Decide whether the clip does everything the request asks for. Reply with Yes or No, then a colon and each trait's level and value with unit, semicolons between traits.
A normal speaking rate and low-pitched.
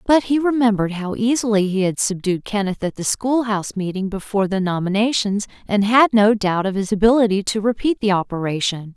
No: average, 190 wpm; high, 210 Hz